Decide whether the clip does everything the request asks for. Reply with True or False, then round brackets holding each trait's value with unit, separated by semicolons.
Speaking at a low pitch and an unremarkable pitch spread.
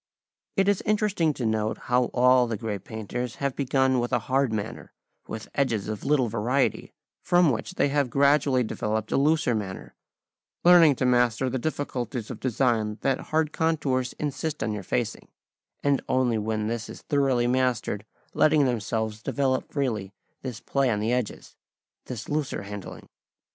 True (125 Hz; 4.1 semitones)